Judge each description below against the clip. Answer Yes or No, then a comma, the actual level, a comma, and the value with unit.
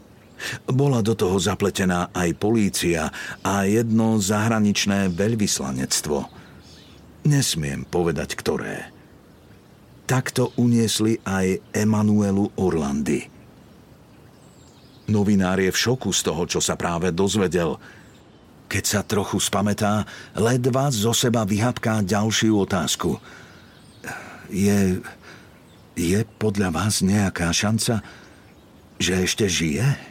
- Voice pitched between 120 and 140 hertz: No, low, 105 Hz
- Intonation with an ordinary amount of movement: Yes, average, 3.0 semitones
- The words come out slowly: Yes, slow, 95 wpm